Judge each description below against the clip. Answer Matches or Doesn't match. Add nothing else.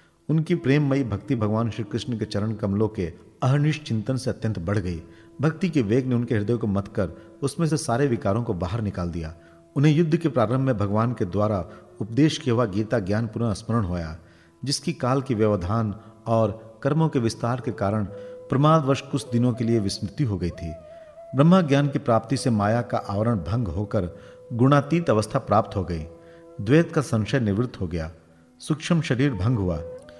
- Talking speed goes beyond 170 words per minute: Matches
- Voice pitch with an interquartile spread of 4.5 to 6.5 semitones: Matches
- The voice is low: Matches